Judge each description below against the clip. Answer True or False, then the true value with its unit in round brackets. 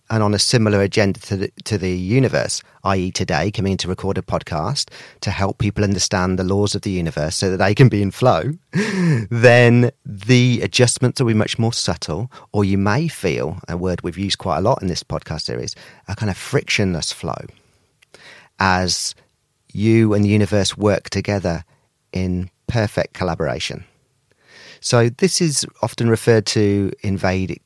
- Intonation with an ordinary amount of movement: True (3.5 semitones)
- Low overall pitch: True (100 Hz)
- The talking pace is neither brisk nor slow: True (175 wpm)